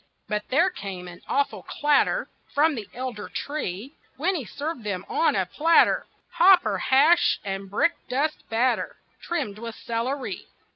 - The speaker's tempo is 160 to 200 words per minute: No, average, 145 wpm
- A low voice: No, very high, 260 Hz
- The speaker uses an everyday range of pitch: No, wide, 7.0 semitones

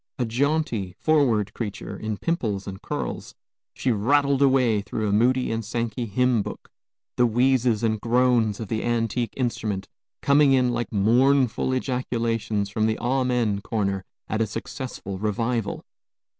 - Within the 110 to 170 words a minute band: Yes, average, 145 wpm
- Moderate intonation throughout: Yes, average, 3.1 semitones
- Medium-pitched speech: No, low, 115 Hz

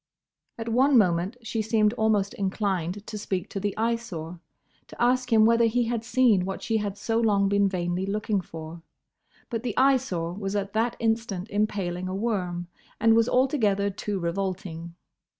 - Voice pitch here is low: No, high, 205 Hz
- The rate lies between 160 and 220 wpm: Yes, average, 170 wpm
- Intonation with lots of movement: No, average, 3.4 semitones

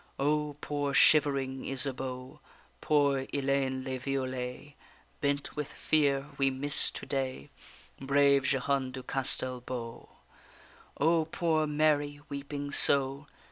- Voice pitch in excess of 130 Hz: Yes, medium, 140 Hz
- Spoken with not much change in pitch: Yes, narrow, 1.7 semitones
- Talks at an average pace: No, slow, 110 wpm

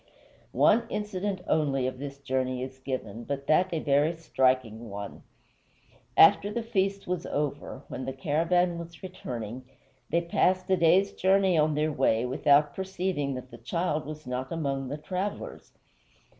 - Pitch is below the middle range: No, medium, 150 Hz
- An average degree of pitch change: No, wide, 5.7 semitones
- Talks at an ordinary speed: Yes, average, 155 wpm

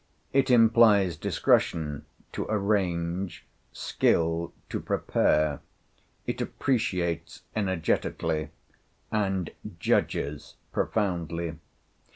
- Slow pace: Yes, slow, 70 wpm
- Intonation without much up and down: No, average, 4.1 semitones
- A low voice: Yes, very low, 90 Hz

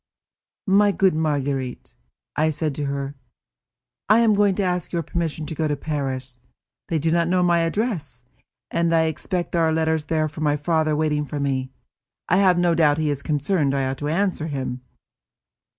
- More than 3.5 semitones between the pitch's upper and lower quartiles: No, average, 3.1 semitones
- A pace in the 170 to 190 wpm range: Yes, average, 180 wpm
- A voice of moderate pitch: Yes, medium, 155 Hz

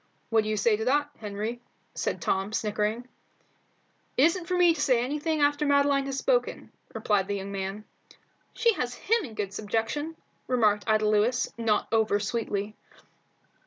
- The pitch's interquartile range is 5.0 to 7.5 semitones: Yes, wide, 5.4 semitones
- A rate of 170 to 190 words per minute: No, average, 160 wpm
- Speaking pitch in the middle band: No, high, 225 Hz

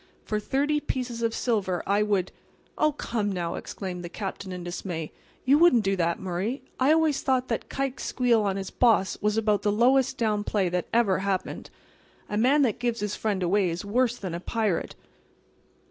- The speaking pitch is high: Yes, high, 210 Hz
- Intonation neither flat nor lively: Yes, average, 4.5 semitones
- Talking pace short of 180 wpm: No, average, 190 wpm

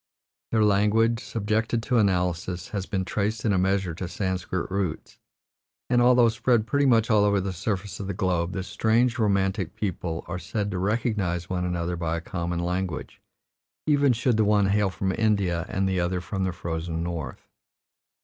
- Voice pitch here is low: Yes, very low, 95 Hz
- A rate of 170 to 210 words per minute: Yes, average, 180 wpm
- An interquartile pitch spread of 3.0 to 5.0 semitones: Yes, average, 3.5 semitones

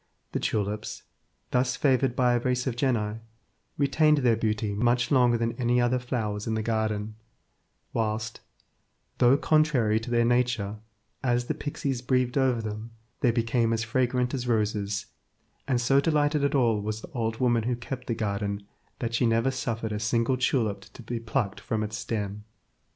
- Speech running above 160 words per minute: Yes, average, 170 wpm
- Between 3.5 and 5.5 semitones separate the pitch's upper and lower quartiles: No, average, 2.7 semitones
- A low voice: Yes, low, 120 Hz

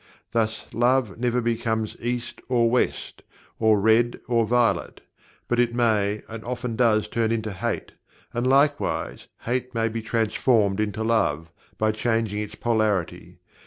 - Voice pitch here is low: Yes, low, 115 Hz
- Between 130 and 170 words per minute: Yes, average, 140 wpm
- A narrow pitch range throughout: Yes, narrow, 1.9 semitones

